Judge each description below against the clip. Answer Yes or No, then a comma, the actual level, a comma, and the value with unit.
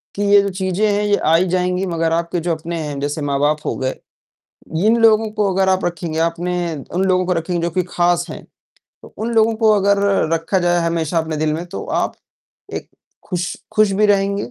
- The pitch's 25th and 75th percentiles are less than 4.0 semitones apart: Yes, average, 3.2 semitones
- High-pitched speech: No, medium, 180 Hz